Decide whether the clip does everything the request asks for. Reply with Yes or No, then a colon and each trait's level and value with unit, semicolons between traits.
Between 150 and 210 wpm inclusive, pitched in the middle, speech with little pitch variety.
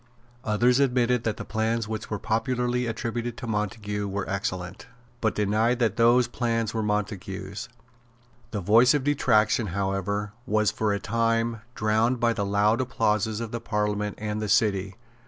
No: average, 155 wpm; low, 110 Hz; narrow, 2.1 semitones